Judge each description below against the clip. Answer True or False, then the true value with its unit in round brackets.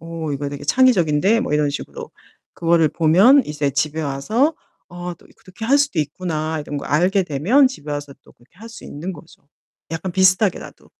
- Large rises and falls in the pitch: False (4.7 semitones)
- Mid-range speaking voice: True (165 Hz)